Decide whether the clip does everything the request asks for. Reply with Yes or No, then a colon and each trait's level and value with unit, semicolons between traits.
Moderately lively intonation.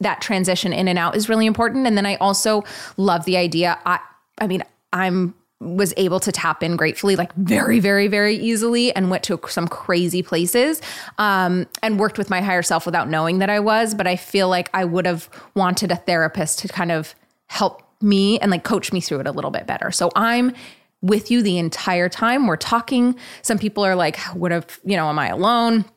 Yes: average, 3.4 semitones